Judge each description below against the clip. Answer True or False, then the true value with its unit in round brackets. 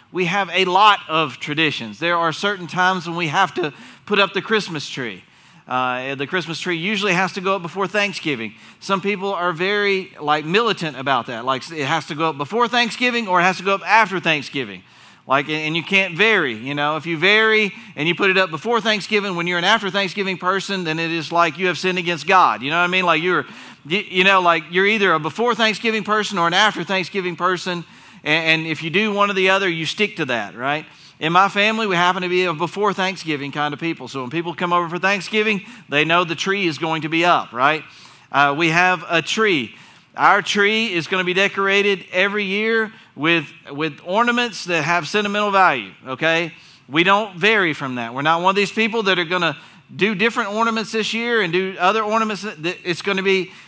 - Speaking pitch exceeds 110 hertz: True (185 Hz)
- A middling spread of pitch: True (3.7 semitones)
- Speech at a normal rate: False (225 wpm)